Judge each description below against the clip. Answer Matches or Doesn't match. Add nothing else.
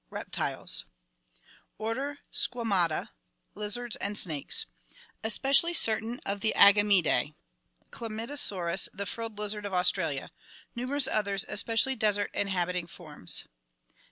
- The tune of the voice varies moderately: Matches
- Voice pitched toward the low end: Doesn't match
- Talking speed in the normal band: Doesn't match